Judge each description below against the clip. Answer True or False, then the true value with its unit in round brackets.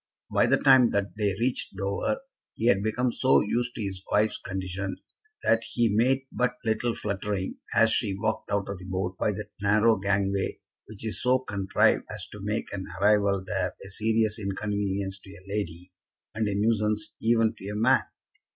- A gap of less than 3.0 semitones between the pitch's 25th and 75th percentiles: True (2.4 semitones)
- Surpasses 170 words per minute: True (180 wpm)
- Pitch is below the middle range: True (105 Hz)